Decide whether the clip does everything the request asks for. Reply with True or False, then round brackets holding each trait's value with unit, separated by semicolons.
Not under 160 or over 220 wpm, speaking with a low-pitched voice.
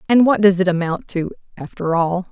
False (205 wpm; 185 Hz)